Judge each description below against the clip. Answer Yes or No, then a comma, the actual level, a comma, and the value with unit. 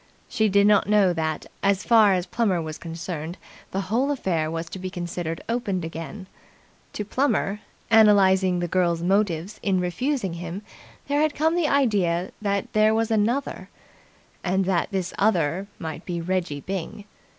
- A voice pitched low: No, high, 190 Hz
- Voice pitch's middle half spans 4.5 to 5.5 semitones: No, average, 3.7 semitones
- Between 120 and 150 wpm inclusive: No, average, 160 wpm